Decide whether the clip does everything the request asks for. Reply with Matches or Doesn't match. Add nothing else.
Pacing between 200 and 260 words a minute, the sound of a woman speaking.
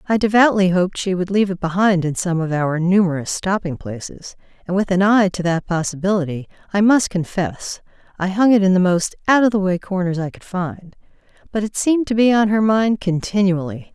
Matches